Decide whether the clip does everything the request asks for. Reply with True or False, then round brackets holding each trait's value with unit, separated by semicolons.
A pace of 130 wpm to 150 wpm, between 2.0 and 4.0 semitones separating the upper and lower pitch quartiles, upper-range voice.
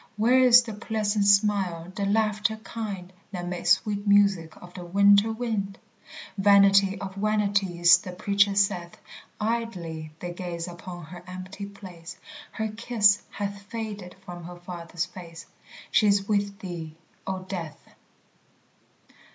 True (135 wpm; 2.8 semitones; 195 Hz)